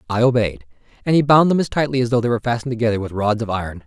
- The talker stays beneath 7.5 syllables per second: No, 7.9 syllables/s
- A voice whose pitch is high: No, low, 120 Hz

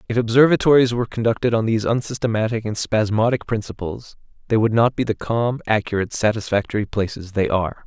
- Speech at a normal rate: Yes, average, 160 wpm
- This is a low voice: Yes, low, 110 Hz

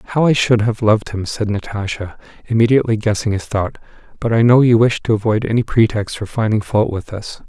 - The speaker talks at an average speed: No, fast, 210 wpm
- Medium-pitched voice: No, low, 110 Hz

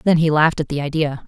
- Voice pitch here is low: No, medium, 155 Hz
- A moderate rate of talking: No, fast, 285 wpm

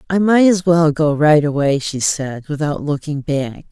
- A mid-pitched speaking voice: Yes, medium, 155 Hz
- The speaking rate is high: No, average, 195 wpm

